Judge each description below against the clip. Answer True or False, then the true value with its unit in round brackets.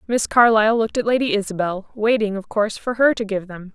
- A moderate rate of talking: False (225 wpm)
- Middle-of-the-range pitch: False (215 Hz)